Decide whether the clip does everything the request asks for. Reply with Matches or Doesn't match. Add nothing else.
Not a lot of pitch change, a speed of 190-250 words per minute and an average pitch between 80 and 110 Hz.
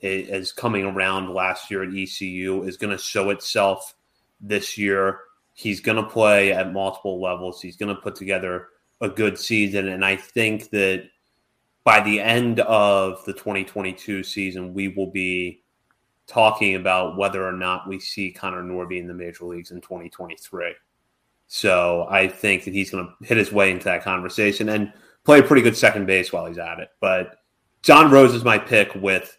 Doesn't match